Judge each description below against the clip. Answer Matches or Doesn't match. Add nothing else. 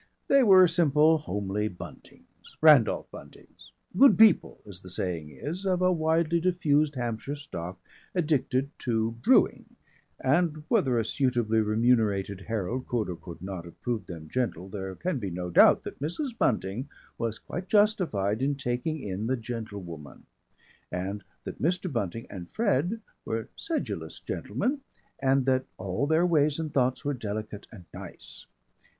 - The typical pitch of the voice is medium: Doesn't match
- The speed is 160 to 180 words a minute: Doesn't match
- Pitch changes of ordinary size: Doesn't match